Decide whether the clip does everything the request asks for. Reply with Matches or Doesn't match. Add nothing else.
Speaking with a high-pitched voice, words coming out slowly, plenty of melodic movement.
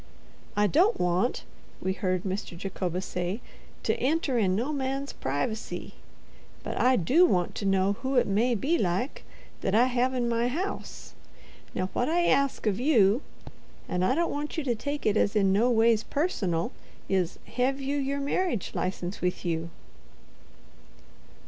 Doesn't match